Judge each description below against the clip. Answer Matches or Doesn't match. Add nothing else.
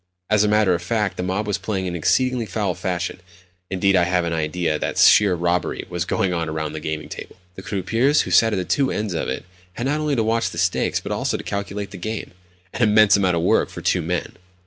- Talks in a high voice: Doesn't match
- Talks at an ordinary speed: Doesn't match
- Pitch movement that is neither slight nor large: Matches